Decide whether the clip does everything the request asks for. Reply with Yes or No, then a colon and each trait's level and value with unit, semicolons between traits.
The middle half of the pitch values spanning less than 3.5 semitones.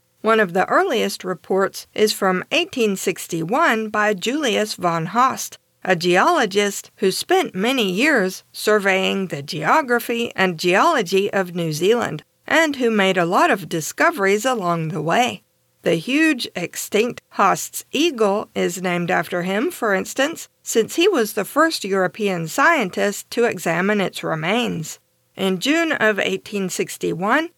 No: average, 4.5 semitones